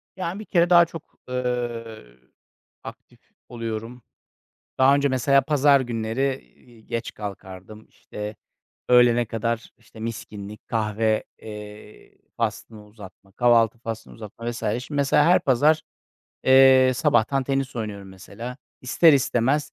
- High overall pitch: No, low, 120 Hz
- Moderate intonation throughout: Yes, average, 3.7 semitones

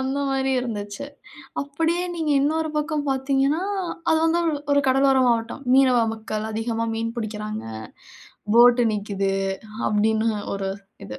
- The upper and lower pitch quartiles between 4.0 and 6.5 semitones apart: Yes, average, 4.4 semitones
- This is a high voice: Yes, high, 245 Hz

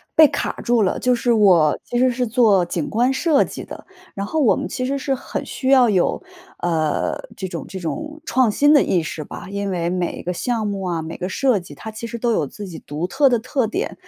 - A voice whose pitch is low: No, high, 220 Hz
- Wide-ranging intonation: Yes, wide, 6.0 semitones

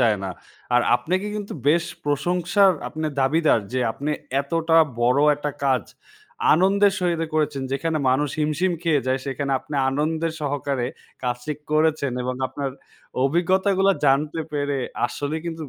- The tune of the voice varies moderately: Yes, average, 3.4 semitones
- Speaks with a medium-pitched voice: Yes, medium, 150 Hz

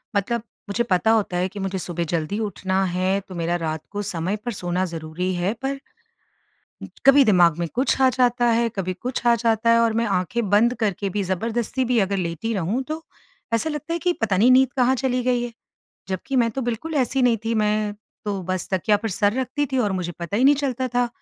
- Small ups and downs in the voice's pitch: No, average, 4.8 semitones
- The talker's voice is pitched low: No, high, 220 Hz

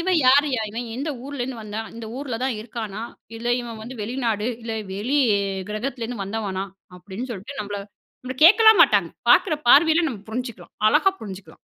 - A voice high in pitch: Yes, high, 235 Hz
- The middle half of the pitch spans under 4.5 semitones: Yes, average, 4.1 semitones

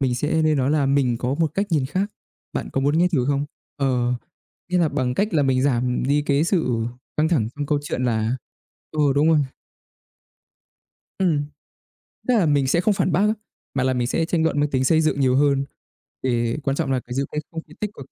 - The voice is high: No, medium, 145 Hz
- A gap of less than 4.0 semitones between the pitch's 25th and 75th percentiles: Yes, average, 3.6 semitones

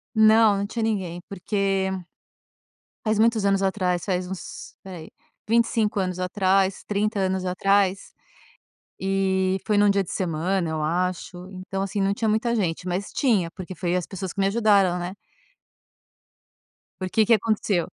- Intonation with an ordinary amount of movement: No, narrow, 2.1 semitones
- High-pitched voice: Yes, high, 195 Hz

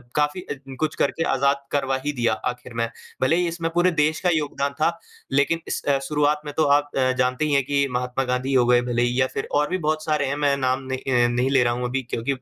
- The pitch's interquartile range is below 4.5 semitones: Yes, average, 2.8 semitones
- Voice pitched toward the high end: No, medium, 140 Hz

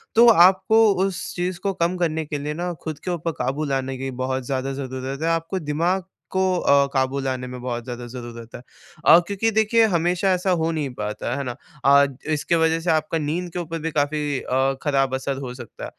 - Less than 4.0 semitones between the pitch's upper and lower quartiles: No, average, 4.8 semitones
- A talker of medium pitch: Yes, medium, 150 Hz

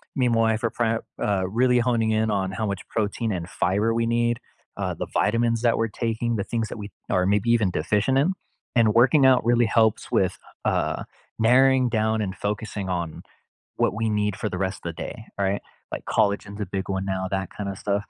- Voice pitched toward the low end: Yes, low, 110 Hz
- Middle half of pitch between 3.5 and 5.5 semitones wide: No, average, 2.9 semitones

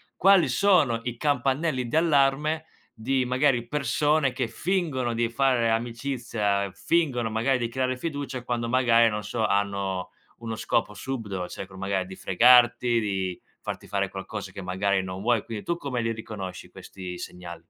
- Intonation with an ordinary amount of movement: Yes, average, 4.7 semitones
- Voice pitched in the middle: No, low, 120 Hz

